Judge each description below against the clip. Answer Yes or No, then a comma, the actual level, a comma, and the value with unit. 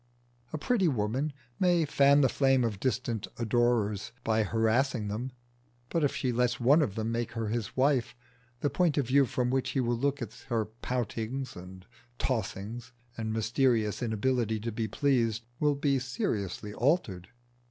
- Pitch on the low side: Yes, low, 120 Hz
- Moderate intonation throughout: Yes, average, 3.5 semitones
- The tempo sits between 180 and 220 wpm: No, average, 165 wpm